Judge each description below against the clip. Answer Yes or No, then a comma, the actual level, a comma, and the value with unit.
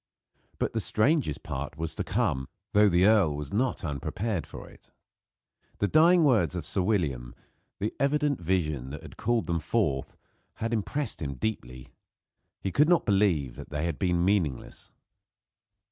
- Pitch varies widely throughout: Yes, wide, 6.9 semitones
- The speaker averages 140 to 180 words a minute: Yes, average, 155 wpm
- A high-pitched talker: No, very low, 90 Hz